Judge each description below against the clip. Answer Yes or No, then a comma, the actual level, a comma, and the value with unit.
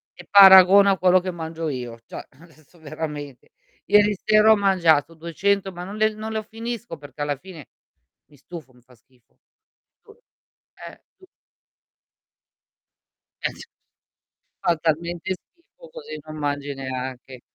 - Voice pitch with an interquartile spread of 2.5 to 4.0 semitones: No, wide, 5.7 semitones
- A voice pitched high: No, medium, 170 Hz